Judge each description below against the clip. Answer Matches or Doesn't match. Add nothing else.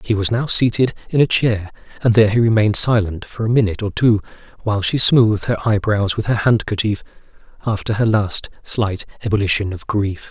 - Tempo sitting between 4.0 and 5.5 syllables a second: Doesn't match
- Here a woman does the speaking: Doesn't match